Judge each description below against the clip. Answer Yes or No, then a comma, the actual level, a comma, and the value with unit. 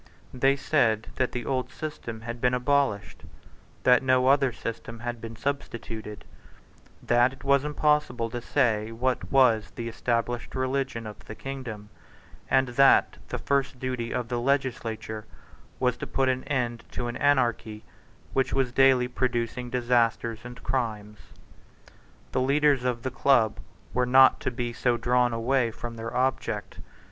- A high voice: No, low, 125 Hz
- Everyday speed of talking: Yes, average, 150 wpm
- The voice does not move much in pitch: Yes, narrow, 2.3 semitones